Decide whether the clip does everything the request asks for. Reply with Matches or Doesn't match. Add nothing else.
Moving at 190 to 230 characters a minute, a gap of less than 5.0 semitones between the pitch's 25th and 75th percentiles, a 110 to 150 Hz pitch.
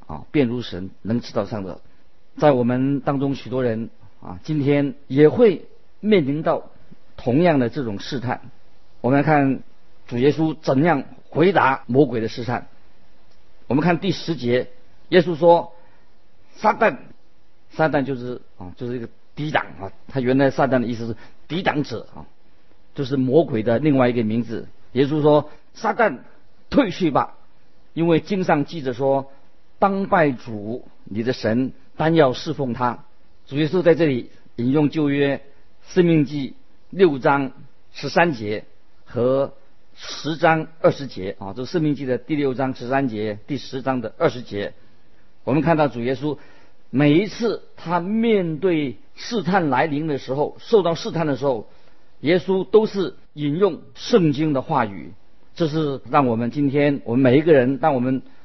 Matches